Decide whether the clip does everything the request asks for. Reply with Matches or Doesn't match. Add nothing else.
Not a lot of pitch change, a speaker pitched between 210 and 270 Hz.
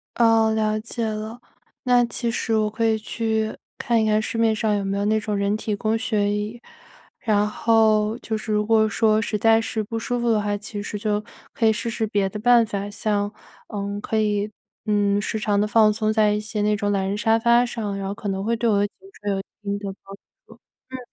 Matches